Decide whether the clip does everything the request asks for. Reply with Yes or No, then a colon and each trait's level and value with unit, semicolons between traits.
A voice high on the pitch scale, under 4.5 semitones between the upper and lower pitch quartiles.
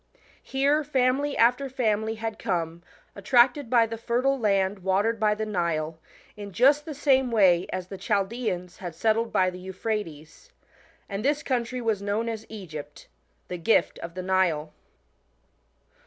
No: high, 215 Hz; average, 5.0 semitones